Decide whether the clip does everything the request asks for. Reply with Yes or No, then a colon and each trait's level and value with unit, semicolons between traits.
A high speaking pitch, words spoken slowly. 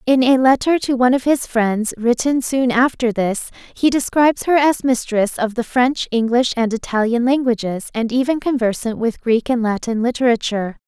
No: high, 240 Hz; average, 175 wpm